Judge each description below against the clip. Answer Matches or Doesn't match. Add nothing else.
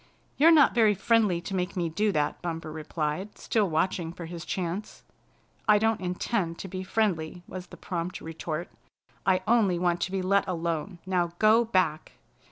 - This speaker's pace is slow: Doesn't match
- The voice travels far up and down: Doesn't match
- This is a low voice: Doesn't match